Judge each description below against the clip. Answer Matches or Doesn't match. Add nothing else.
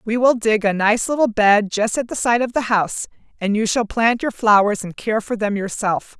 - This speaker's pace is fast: Matches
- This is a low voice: Doesn't match